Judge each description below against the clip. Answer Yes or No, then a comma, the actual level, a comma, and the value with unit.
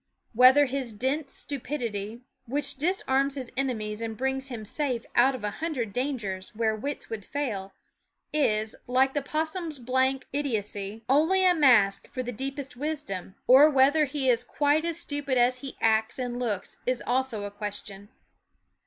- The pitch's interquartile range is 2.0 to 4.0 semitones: No, average, 4.4 semitones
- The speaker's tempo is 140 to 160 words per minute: No, average, 170 wpm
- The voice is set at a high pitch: Yes, very high, 255 Hz